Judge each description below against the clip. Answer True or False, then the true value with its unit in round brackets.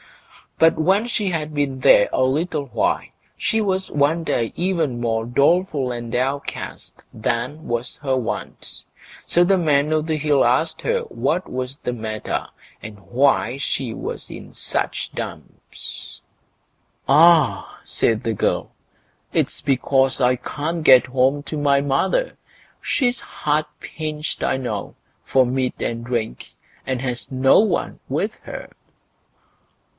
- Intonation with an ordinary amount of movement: True (4.2 semitones)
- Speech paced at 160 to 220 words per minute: False (140 wpm)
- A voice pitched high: False (140 Hz)